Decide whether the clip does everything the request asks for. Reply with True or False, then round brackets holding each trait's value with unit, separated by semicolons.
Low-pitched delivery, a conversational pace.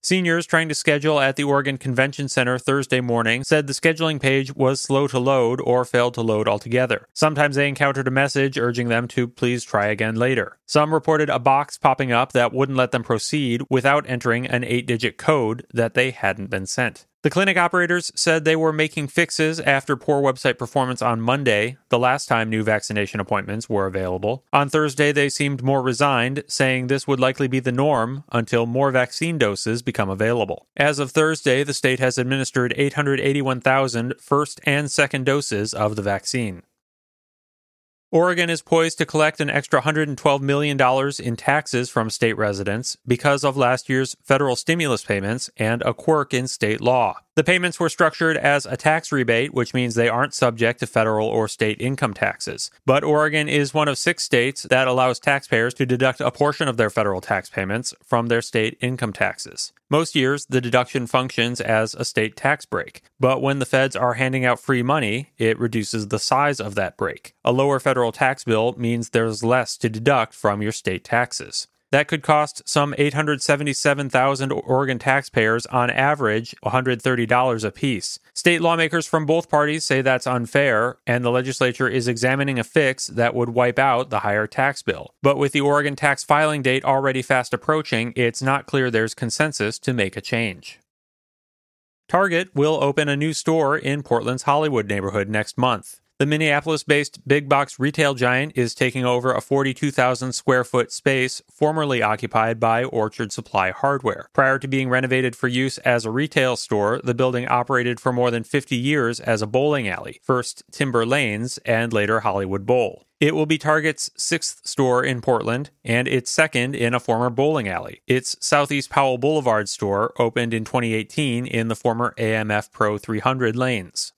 True (130 Hz; 180 wpm)